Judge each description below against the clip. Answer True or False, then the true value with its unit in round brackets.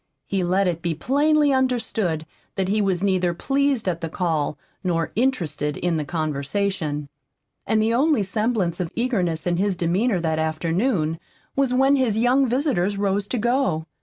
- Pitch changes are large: True (6.7 semitones)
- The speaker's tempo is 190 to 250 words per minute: False (165 wpm)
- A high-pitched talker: True (195 Hz)